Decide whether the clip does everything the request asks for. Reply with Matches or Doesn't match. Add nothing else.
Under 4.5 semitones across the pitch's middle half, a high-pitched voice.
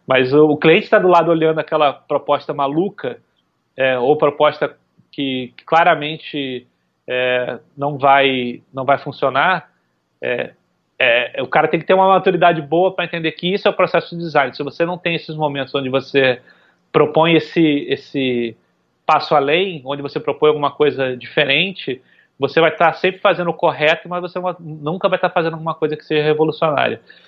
Doesn't match